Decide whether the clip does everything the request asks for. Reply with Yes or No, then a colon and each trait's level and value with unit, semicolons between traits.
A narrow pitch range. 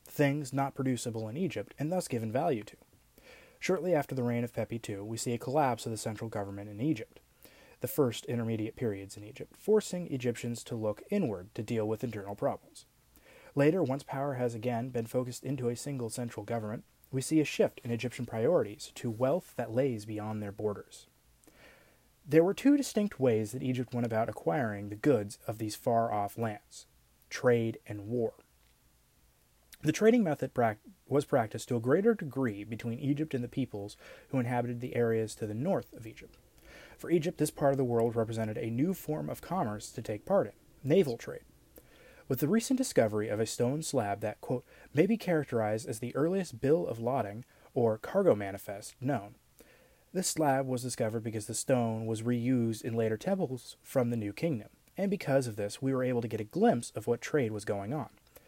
No: average, 4.0 semitones